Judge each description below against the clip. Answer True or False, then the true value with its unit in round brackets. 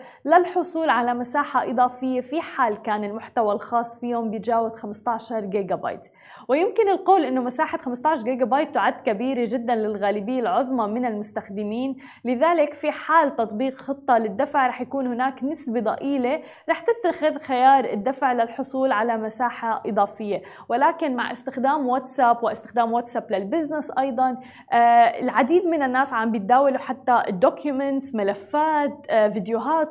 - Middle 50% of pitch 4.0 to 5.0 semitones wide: False (3.3 semitones)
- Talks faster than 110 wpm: True (130 wpm)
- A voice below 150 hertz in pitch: False (255 Hz)